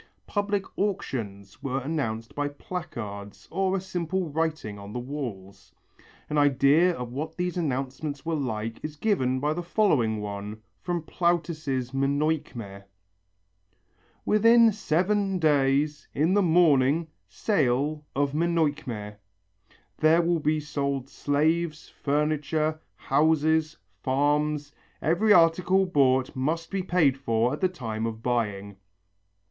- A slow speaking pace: Yes, slow, 120 wpm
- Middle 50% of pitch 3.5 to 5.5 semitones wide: Yes, average, 4.7 semitones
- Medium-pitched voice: Yes, medium, 150 Hz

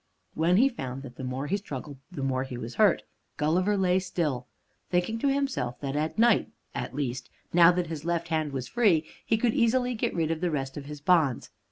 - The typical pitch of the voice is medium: Yes, medium, 160 Hz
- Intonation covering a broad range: Yes, wide, 5.8 semitones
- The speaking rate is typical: No, fast, 215 wpm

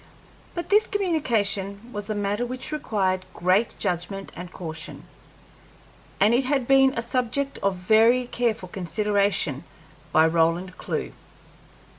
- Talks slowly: Yes, slow, 125 wpm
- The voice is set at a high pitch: Yes, high, 205 Hz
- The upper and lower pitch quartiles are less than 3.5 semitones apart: No, average, 4.9 semitones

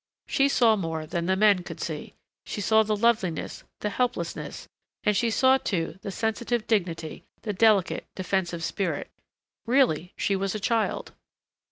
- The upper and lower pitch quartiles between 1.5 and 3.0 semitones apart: No, average, 4.2 semitones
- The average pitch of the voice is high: Yes, high, 200 Hz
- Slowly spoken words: No, average, 155 wpm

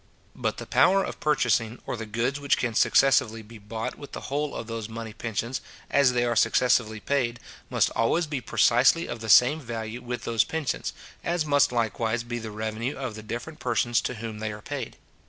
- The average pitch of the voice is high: No, low, 120 Hz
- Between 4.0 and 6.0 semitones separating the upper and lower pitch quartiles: No, average, 3.2 semitones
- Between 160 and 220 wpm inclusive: Yes, average, 200 wpm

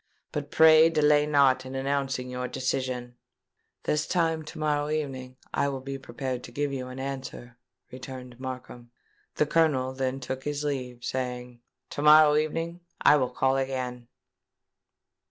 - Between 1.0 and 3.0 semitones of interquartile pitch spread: Yes, narrow, 2.6 semitones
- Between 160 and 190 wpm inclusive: No, average, 150 wpm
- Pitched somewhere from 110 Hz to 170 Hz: Yes, low, 135 Hz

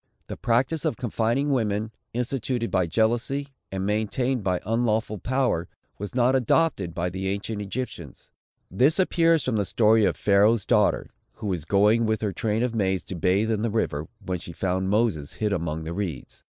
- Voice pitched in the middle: No, low, 110 Hz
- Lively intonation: No, average, 4.1 semitones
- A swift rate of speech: No, average, 180 wpm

